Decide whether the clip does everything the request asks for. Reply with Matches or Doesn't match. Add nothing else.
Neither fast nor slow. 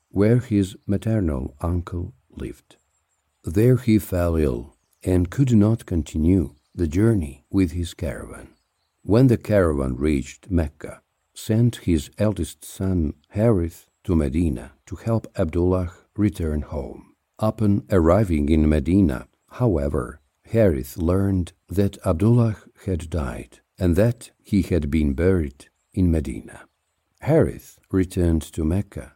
Doesn't match